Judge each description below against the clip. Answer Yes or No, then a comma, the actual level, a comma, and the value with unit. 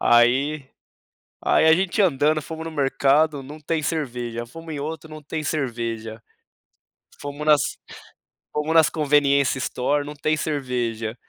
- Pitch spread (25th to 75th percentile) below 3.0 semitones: No, average, 3.3 semitones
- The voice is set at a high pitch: No, medium, 145 Hz